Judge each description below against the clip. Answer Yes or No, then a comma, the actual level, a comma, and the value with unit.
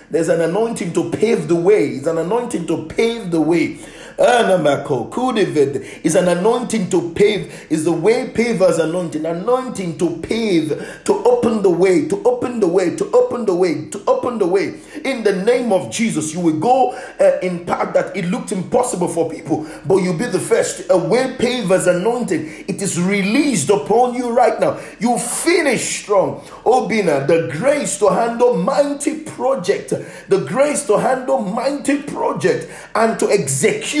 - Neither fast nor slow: Yes, average, 170 wpm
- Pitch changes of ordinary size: No, wide, 7.1 semitones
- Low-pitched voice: No, high, 225 Hz